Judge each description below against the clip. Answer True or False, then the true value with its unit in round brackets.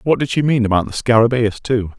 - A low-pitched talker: True (115 Hz)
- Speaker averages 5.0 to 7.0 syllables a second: True (5.9 syllables/s)